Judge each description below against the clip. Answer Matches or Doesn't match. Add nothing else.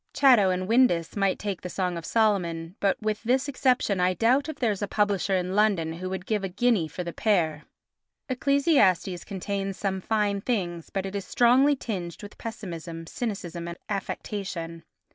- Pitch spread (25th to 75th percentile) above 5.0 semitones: Doesn't match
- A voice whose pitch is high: Matches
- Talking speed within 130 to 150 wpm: Doesn't match